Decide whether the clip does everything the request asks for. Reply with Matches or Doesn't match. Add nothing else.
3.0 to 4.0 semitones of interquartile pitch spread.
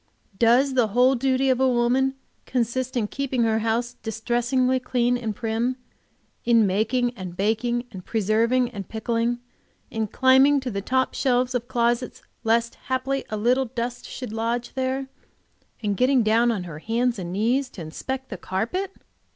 Doesn't match